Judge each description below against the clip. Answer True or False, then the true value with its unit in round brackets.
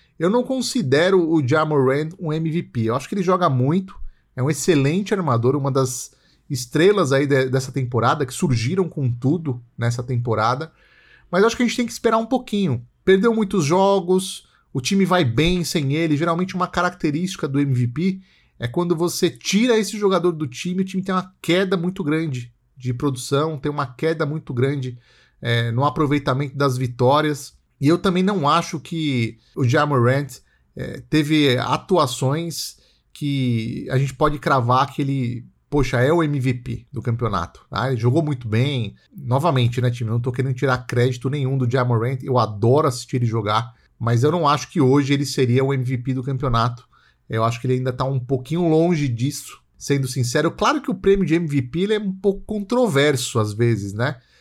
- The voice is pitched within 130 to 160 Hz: True (140 Hz)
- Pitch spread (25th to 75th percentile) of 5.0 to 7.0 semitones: True (5.5 semitones)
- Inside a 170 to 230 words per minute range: True (185 wpm)